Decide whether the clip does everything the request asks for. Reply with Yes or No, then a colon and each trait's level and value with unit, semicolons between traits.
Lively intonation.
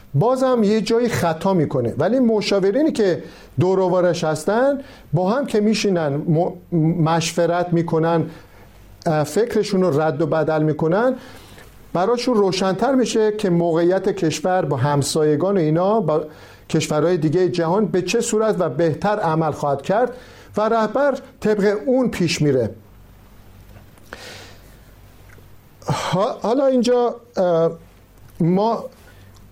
Yes: wide, 6.6 semitones